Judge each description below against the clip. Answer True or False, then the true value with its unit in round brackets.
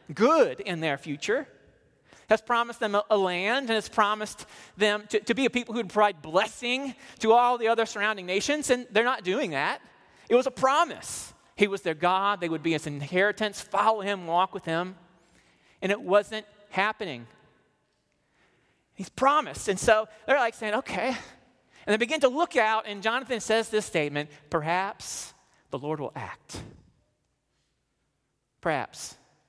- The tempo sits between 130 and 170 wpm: True (165 wpm)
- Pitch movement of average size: True (4.1 semitones)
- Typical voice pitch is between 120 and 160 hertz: False (210 Hz)